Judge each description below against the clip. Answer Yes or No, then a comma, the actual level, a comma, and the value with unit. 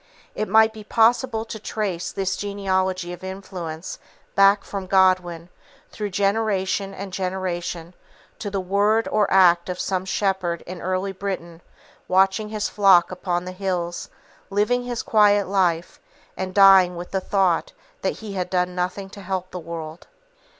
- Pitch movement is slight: Yes, narrow, 2.0 semitones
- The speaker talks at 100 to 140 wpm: No, average, 150 wpm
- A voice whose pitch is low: No, high, 190 Hz